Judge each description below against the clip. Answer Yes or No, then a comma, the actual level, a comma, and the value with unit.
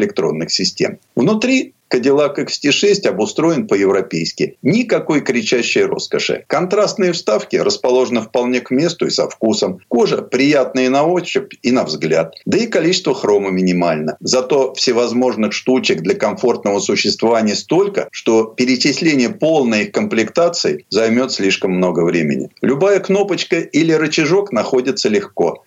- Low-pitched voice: Yes, low, 130 Hz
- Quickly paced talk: No, average, 125 wpm